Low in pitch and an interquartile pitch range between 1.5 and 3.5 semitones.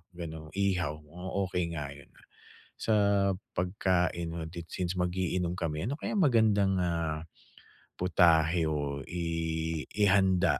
Yes: very low, 85 Hz; narrow, 2.5 semitones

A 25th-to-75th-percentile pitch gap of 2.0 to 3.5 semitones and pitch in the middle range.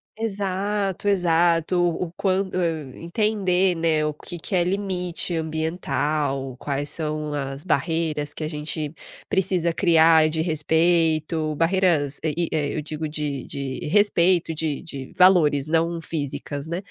Yes: average, 2.9 semitones; medium, 165 Hz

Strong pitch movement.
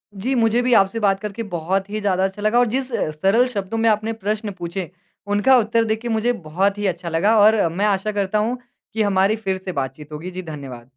No: average, 3.1 semitones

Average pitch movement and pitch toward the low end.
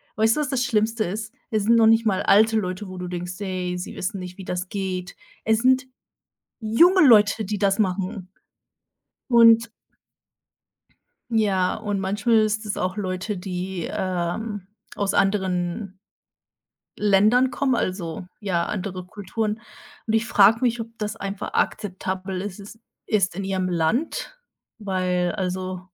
No: average, 3.1 semitones; high, 200 Hz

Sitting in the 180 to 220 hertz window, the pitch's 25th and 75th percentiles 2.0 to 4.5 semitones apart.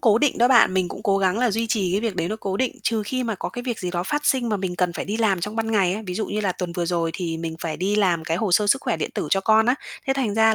Yes: high, 205 Hz; average, 3.8 semitones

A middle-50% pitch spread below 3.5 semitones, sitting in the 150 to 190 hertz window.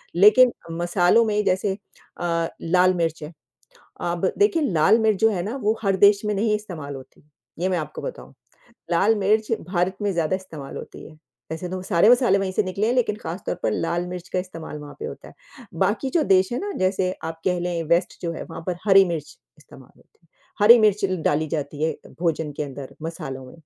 No: average, 4.0 semitones; medium, 185 Hz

